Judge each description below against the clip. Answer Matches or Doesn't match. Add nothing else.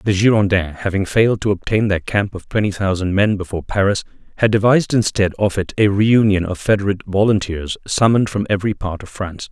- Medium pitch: Doesn't match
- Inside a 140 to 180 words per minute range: Doesn't match